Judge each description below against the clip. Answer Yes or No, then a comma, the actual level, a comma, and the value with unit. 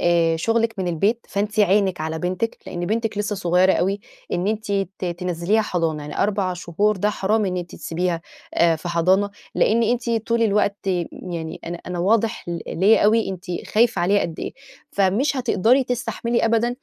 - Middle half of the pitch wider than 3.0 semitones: Yes, average, 4.1 semitones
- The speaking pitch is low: No, high, 200 Hz